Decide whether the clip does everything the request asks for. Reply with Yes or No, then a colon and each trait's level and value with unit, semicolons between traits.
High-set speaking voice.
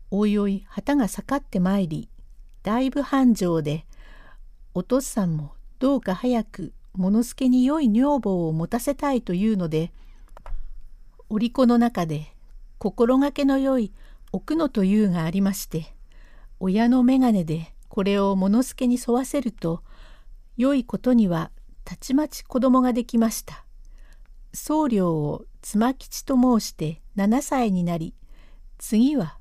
Yes: high, 220 Hz